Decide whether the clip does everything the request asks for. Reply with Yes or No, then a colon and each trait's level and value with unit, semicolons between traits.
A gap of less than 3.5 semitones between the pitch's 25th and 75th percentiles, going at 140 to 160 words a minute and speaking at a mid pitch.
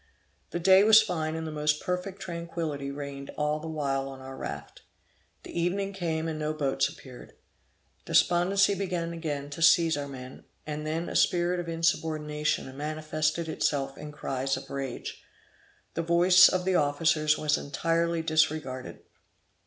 Yes: average, 2.8 semitones; average, 155 wpm; medium, 155 Hz